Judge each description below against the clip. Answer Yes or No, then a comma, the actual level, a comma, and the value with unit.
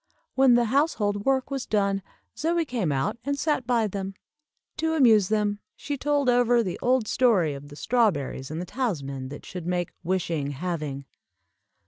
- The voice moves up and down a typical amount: No, wide, 6.9 semitones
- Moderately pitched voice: No, high, 210 Hz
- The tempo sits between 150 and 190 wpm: Yes, average, 165 wpm